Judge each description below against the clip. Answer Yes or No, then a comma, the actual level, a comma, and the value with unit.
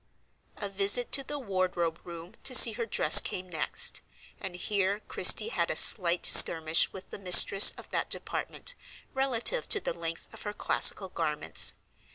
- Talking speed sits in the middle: Yes, average, 165 wpm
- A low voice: No, high, 195 Hz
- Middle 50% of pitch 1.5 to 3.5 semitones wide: No, average, 5.0 semitones